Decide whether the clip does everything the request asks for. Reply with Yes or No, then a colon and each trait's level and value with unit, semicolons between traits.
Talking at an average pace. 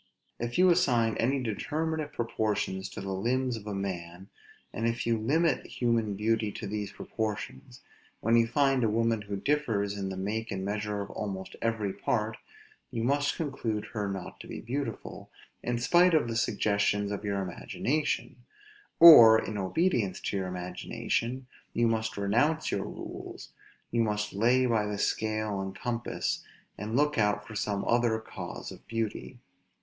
Yes: average, 165 wpm